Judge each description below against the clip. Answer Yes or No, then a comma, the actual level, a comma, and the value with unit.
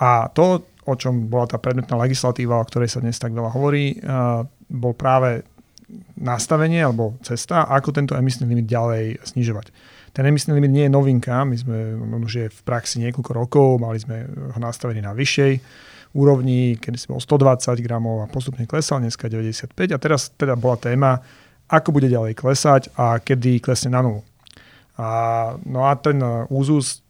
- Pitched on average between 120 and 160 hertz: Yes, low, 125 Hz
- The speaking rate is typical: No, fast, 170 wpm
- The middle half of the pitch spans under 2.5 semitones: No, average, 2.8 semitones